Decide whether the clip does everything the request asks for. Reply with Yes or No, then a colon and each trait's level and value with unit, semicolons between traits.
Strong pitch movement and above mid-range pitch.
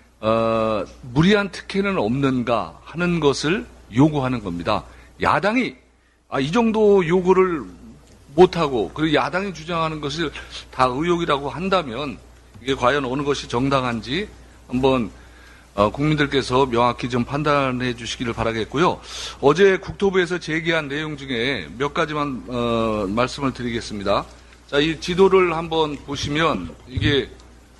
No: wide, 6.0 semitones; medium, 140 Hz